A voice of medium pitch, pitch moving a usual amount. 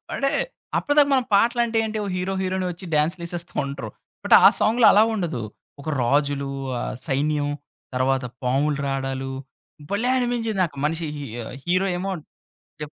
No: medium, 170 Hz; wide, 7.5 semitones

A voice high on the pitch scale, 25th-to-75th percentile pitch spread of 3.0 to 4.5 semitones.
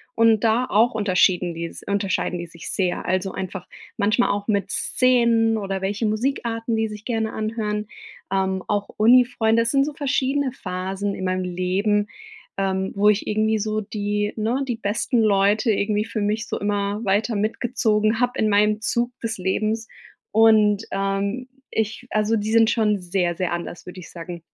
No: high, 210 Hz; narrow, 2.4 semitones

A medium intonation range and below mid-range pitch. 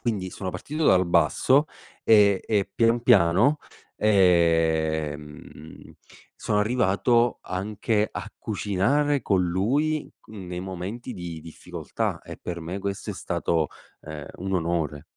Yes: average, 4.7 semitones; very low, 95 Hz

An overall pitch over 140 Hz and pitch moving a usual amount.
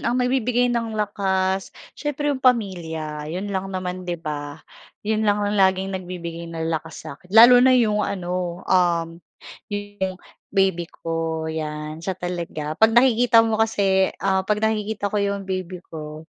Yes: high, 190 Hz; average, 4.2 semitones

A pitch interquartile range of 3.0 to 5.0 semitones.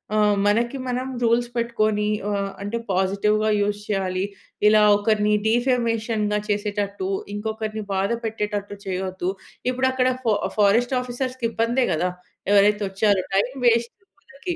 No: narrow, 2.6 semitones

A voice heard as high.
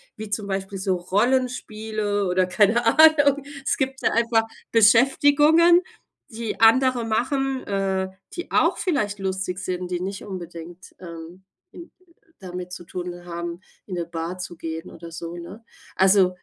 Yes: high, 195 Hz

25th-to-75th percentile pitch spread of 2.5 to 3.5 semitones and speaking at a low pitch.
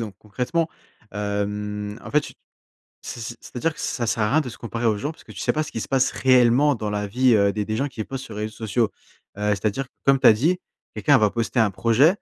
No: average, 4.3 semitones; low, 115 Hz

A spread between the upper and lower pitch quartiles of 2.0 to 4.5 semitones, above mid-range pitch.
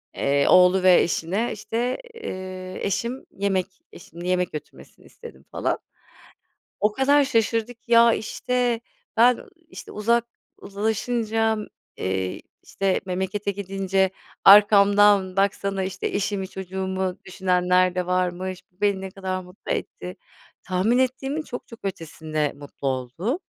Yes: average, 3.4 semitones; high, 195 Hz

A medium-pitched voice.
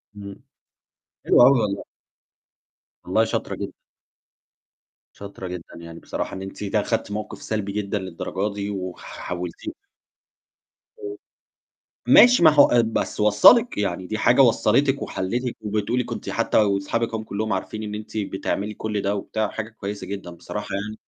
No: low, 105 Hz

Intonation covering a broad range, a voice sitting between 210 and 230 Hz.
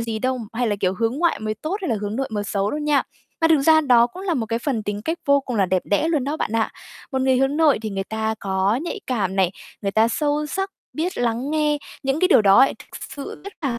No: wide, 5.7 semitones; very high, 250 Hz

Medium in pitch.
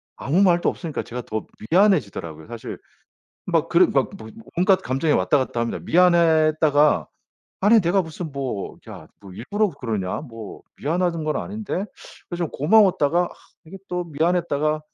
Yes: medium, 155 Hz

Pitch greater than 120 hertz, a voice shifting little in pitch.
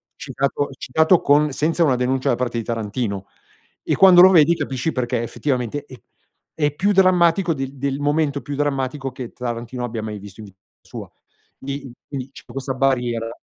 No: low, 135 Hz; average, 3.4 semitones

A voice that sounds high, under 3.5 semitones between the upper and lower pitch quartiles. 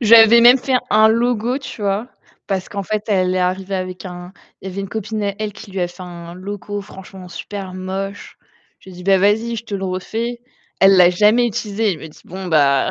Yes: high, 195 Hz; average, 2.9 semitones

